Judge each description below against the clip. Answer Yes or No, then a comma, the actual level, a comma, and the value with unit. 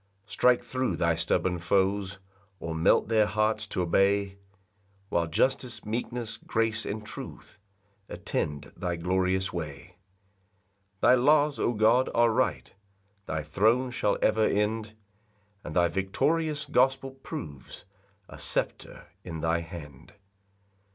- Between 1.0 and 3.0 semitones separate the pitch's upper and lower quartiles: No, wide, 5.6 semitones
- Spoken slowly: Yes, slow, 120 wpm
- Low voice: Yes, low, 100 Hz